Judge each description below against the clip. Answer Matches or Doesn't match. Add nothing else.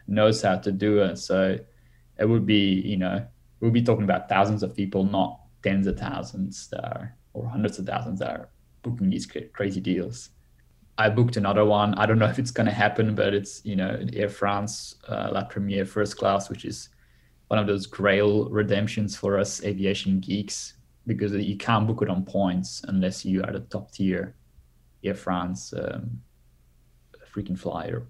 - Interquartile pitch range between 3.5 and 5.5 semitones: Doesn't match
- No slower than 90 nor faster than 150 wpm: Doesn't match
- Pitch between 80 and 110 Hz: Matches